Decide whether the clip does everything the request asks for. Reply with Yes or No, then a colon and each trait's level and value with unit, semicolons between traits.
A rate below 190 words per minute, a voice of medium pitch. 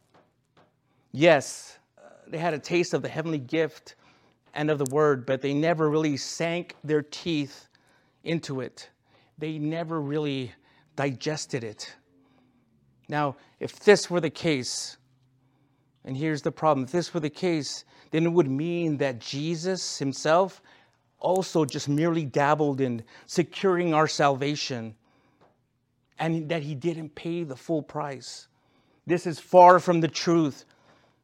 Yes: slow, 135 wpm; medium, 150 Hz